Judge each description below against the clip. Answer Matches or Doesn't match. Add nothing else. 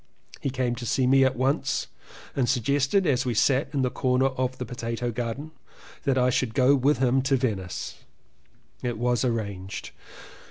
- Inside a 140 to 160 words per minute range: Doesn't match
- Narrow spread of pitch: Matches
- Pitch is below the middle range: Matches